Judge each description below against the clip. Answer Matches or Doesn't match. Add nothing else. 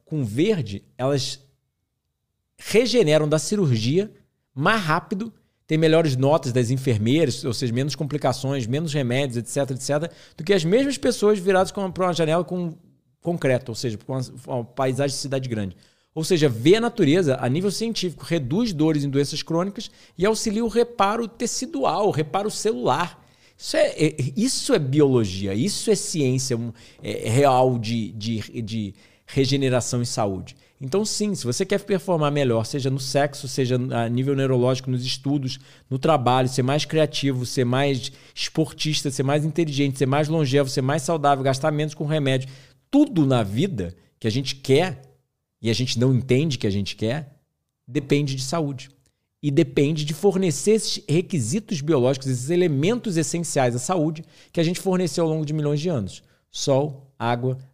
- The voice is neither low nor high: Matches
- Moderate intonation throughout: Matches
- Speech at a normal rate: Matches